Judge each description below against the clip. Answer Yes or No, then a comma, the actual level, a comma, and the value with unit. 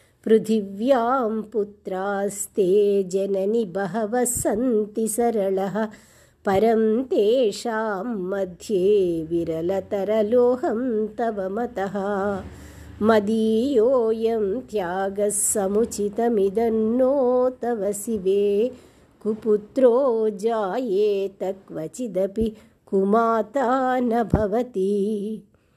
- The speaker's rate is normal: No, slow, 55 wpm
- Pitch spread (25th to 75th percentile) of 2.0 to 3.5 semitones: Yes, average, 2.8 semitones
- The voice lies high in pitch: Yes, high, 215 Hz